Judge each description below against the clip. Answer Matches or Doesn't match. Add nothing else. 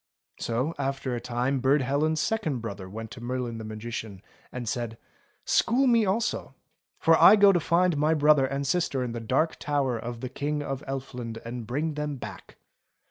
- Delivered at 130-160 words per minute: Doesn't match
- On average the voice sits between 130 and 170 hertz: Matches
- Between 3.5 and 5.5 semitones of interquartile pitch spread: Matches